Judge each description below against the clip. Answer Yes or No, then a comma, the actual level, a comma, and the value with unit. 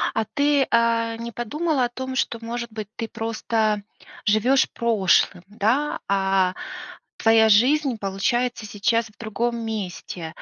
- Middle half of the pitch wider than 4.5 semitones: No, narrow, 2.6 semitones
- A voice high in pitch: Yes, high, 225 Hz